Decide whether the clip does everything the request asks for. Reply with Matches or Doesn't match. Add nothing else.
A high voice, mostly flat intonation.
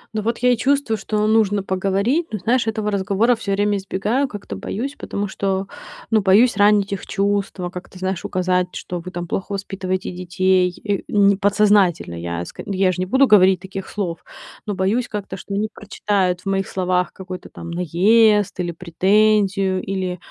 Matches